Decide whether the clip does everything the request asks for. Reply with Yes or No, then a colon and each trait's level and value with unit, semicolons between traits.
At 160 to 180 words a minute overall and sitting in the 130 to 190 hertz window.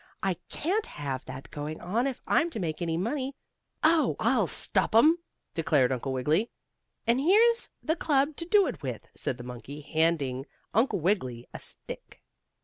Yes: average, 165 wpm; medium, 185 Hz